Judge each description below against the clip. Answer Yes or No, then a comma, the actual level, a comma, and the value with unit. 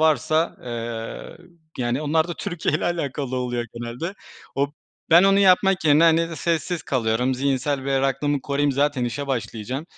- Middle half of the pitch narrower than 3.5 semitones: No, average, 4.3 semitones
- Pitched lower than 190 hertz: Yes, medium, 140 Hz